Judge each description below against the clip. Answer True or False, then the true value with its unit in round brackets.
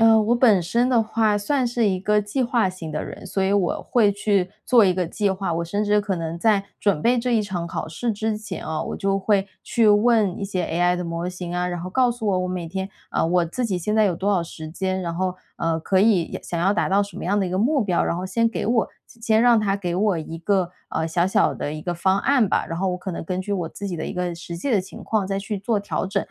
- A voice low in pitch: False (195 Hz)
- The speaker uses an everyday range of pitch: True (3.4 semitones)